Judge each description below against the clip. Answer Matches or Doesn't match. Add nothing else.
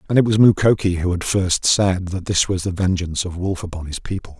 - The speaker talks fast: Matches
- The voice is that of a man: Matches